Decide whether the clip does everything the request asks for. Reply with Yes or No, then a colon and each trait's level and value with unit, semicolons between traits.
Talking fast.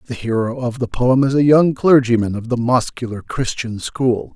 No: average, 195 wpm